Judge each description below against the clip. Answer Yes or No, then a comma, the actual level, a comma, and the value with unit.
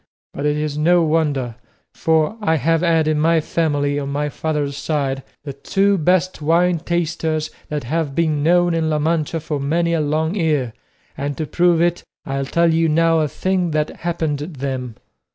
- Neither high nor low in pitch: Yes, medium, 155 Hz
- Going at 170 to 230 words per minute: Yes, average, 180 wpm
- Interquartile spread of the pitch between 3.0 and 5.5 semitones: No, narrow, 2.4 semitones